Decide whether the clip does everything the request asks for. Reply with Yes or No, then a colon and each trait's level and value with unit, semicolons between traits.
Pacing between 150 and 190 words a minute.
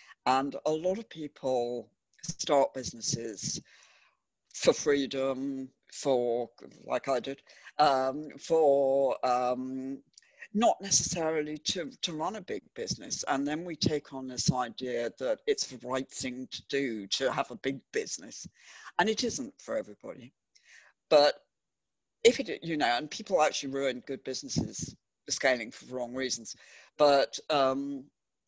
No: average, 140 wpm